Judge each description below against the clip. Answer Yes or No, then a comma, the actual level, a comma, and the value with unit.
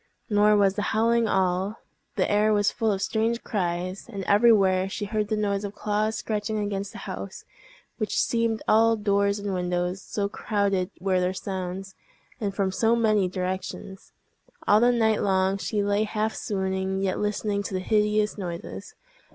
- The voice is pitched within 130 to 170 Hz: No, high, 205 Hz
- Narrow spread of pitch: Yes, narrow, 2.0 semitones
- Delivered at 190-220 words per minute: No, average, 170 wpm